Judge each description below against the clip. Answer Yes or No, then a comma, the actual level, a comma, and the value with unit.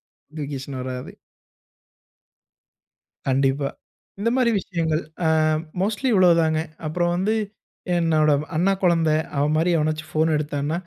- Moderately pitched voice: Yes, medium, 155 Hz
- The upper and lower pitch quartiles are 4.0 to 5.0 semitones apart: No, average, 3.1 semitones